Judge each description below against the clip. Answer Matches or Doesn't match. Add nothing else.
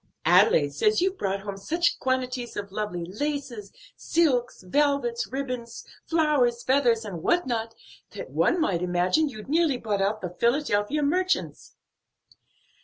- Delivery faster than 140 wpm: Doesn't match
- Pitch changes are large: Matches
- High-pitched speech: Matches